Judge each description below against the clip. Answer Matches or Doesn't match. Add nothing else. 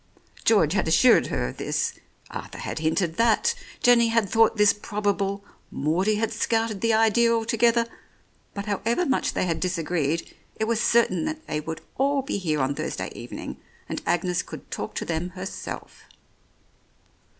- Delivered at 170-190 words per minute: Doesn't match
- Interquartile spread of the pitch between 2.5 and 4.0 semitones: Doesn't match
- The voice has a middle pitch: Doesn't match